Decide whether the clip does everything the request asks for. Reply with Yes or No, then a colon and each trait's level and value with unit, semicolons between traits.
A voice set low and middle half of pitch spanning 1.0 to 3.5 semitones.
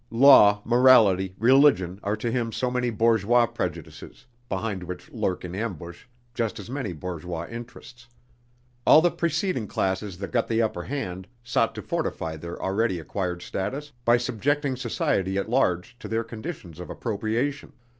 No: low, 110 Hz; average, 4.9 semitones